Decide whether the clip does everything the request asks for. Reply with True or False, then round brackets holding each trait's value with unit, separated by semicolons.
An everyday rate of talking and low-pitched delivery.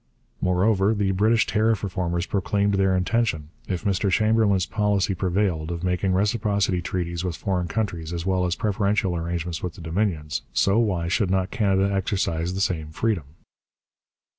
True (155 wpm; 95 Hz)